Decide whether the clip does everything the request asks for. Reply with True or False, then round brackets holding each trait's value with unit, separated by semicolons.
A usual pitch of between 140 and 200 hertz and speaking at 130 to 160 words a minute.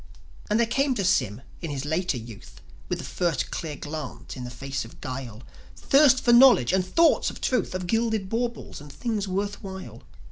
False (185 Hz; 190 wpm)